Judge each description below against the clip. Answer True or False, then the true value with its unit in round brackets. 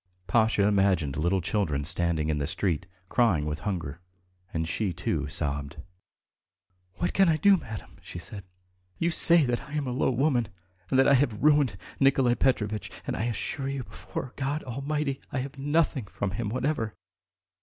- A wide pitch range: True (7.8 semitones)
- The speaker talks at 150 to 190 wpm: True (175 wpm)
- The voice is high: False (115 Hz)